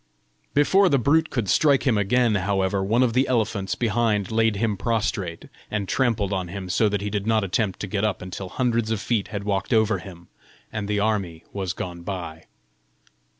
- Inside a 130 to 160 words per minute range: No, average, 190 wpm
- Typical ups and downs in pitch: Yes, average, 3.1 semitones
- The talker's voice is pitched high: No, low, 105 Hz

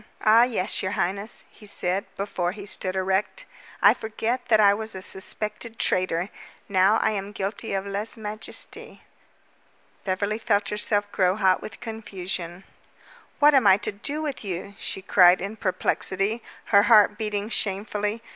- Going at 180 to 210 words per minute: No, average, 155 wpm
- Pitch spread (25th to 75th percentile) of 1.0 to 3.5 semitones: Yes, narrow, 2.4 semitones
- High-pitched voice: Yes, high, 205 Hz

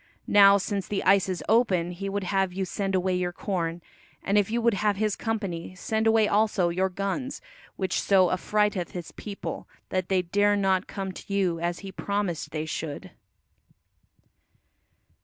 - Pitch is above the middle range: Yes, high, 195 Hz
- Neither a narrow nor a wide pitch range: No, narrow, 2.3 semitones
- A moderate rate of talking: Yes, average, 170 wpm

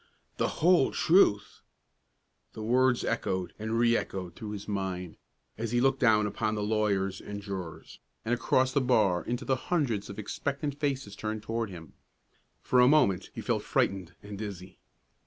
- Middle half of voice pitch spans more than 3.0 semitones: Yes, average, 4.3 semitones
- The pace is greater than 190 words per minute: No, average, 165 wpm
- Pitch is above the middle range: No, low, 110 Hz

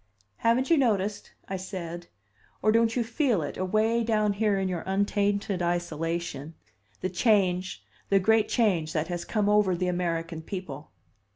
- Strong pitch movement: No, average, 3.7 semitones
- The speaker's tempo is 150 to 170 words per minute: Yes, average, 155 wpm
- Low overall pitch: No, high, 190 Hz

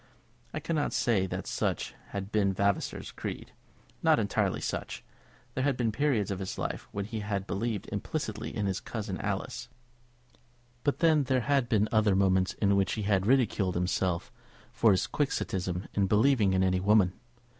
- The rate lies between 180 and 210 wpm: No, average, 165 wpm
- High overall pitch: No, low, 100 Hz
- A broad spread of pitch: No, average, 3.7 semitones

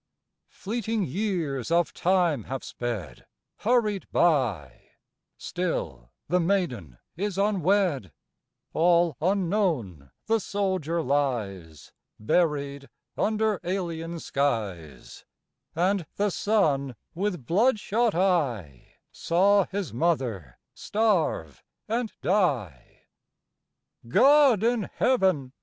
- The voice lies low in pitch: No, medium, 170 Hz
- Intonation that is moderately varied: No, wide, 7.9 semitones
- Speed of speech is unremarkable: No, slow, 90 wpm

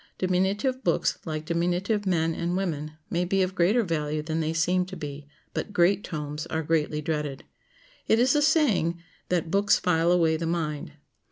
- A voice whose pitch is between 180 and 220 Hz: No, medium, 170 Hz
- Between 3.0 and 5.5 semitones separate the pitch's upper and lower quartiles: Yes, average, 3.3 semitones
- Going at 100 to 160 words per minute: No, average, 175 wpm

